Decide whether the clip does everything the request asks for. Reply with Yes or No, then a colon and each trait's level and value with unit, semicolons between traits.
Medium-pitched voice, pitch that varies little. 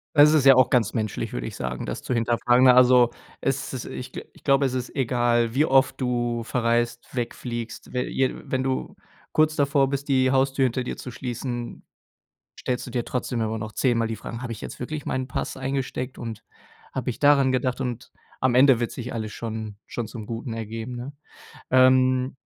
No: low, 125 Hz; narrow, 2.0 semitones